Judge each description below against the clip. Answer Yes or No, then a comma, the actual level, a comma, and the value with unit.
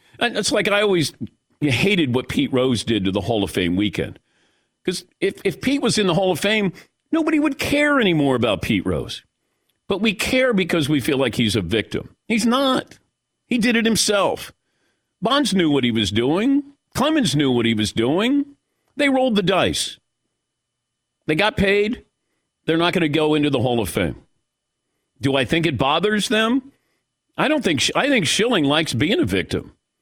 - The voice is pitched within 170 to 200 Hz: Yes, medium, 185 Hz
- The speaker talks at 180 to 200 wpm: Yes, average, 190 wpm